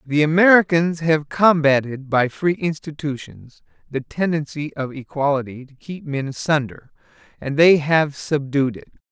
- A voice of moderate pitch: Yes, medium, 150 Hz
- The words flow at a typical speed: No, slow, 130 wpm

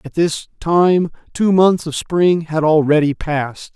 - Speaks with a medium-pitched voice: Yes, medium, 160 Hz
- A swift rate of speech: No, average, 160 wpm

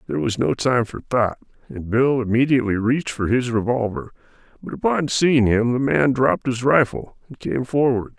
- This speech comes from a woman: No, male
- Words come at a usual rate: Yes, average, 185 wpm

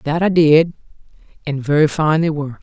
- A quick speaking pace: No, average, 185 wpm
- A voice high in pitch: No, medium, 150 Hz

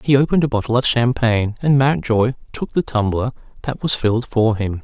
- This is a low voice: Yes, low, 120 Hz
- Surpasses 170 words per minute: Yes, average, 200 wpm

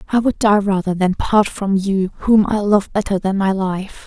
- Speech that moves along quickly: Yes, fast, 220 wpm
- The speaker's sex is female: Yes, female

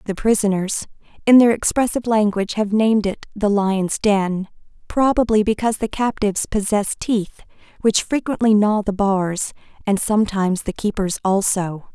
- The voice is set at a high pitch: Yes, high, 205 Hz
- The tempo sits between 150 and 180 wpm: No, average, 140 wpm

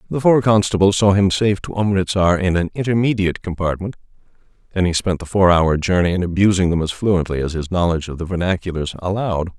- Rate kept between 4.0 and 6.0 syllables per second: No, 6.3 syllables/s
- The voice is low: Yes, very low, 90 Hz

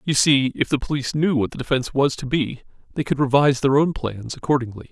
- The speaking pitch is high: No, low, 135 Hz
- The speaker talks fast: Yes, fast, 230 wpm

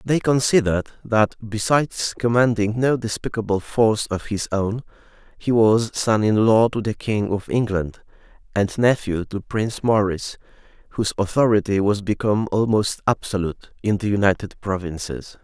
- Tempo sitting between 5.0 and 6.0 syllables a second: Yes, 5.1 syllables/s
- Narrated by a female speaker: No, male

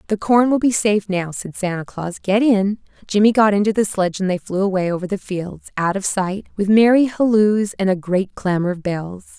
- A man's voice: No, female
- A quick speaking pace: Yes, fast, 225 wpm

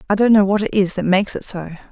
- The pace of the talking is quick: Yes, fast, 315 wpm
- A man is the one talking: No, female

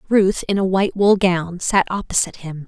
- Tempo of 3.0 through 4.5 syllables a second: No, 5.3 syllables/s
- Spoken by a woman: Yes, female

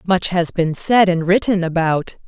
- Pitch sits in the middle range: Yes, medium, 180 Hz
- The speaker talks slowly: No, average, 185 wpm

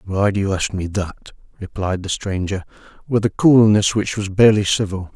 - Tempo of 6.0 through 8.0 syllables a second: No, 5.1 syllables/s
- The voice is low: Yes, low, 100 Hz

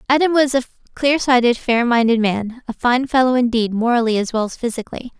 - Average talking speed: Yes, average, 185 wpm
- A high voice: Yes, high, 240 Hz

